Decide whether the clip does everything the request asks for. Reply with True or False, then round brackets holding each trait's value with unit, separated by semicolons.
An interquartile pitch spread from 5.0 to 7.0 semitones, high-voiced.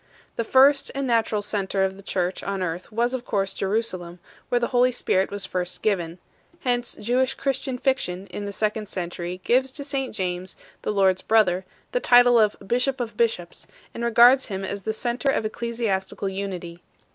False (4.3 semitones; 215 Hz)